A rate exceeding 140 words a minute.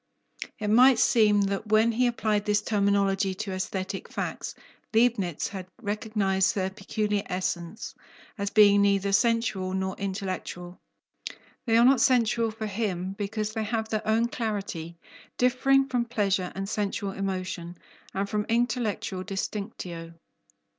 No: slow, 135 wpm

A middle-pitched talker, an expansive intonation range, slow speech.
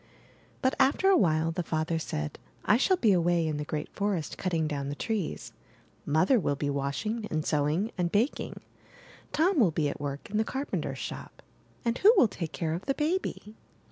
No: medium, 175 Hz; wide, 6.9 semitones; average, 190 wpm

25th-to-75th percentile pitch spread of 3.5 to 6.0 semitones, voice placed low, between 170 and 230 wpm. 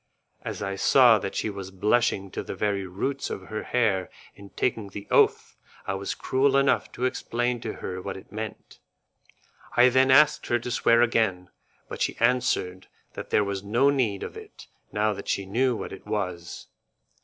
Yes: average, 4.1 semitones; low, 105 Hz; average, 185 wpm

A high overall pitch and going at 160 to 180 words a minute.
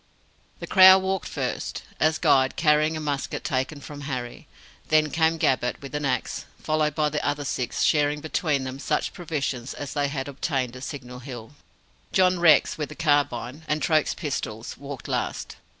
No: medium, 145 Hz; average, 170 wpm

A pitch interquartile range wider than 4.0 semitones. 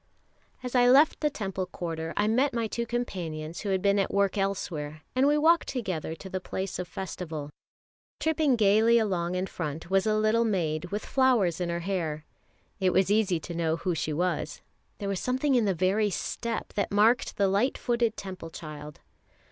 Yes: average, 5.1 semitones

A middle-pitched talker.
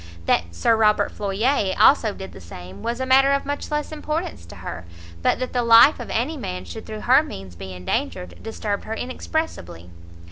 No: high, 225 Hz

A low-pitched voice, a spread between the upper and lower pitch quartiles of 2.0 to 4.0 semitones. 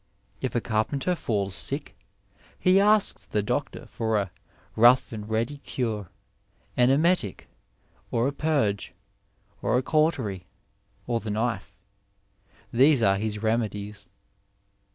No: low, 110 Hz; average, 4.7 semitones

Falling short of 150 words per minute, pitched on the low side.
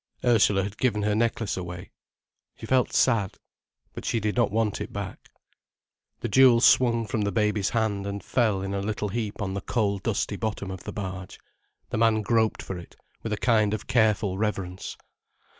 No: average, 185 wpm; low, 105 Hz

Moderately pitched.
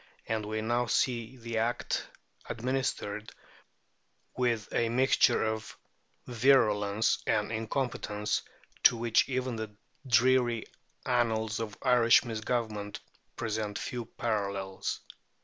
No: low, 115 Hz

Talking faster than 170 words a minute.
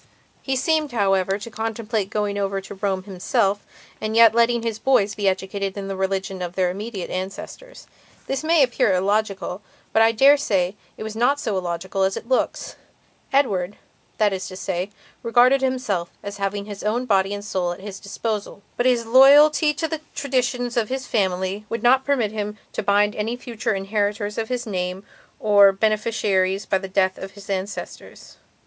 Yes: average, 180 wpm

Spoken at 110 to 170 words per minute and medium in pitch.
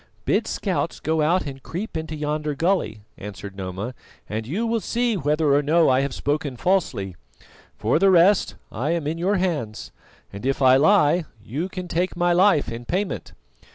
No: average, 180 wpm; medium, 155 Hz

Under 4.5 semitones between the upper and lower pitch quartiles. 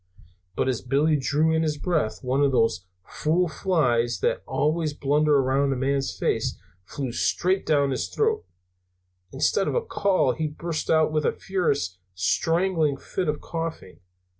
Yes: average, 3.6 semitones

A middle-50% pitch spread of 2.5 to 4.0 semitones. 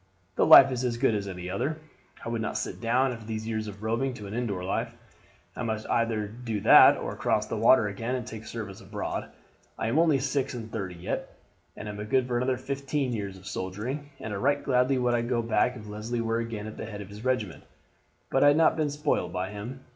Yes: average, 3.4 semitones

